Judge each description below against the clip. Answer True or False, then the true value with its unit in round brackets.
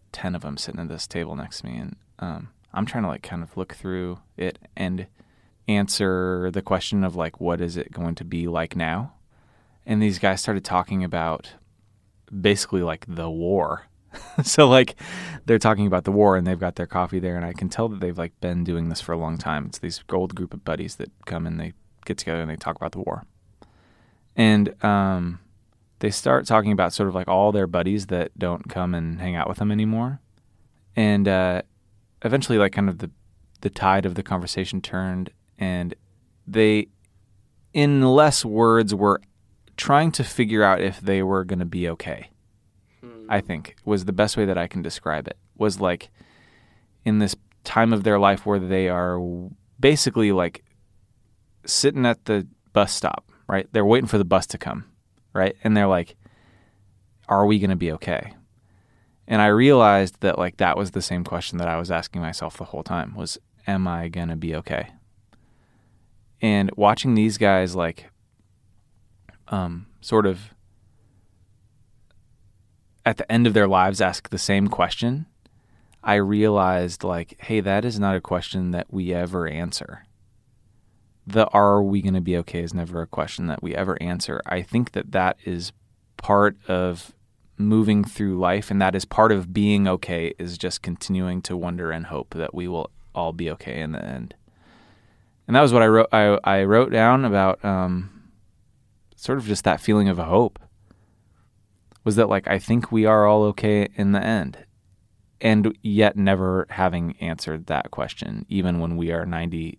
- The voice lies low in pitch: True (100 Hz)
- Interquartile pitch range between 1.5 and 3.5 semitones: True (3.1 semitones)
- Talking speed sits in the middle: True (185 wpm)